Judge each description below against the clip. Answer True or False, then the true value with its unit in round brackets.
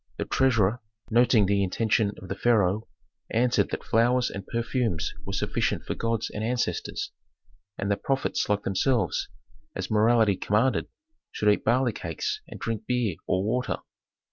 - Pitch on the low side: True (110 Hz)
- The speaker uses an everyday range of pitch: True (3.1 semitones)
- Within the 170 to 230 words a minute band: False (150 wpm)